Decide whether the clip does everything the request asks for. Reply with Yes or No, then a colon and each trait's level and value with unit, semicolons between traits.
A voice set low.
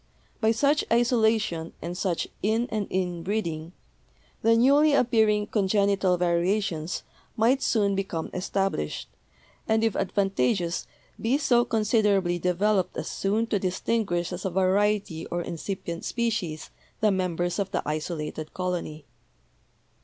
No: high, 195 Hz